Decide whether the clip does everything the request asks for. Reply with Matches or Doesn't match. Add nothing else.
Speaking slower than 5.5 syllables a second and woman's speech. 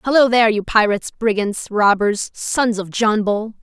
Matches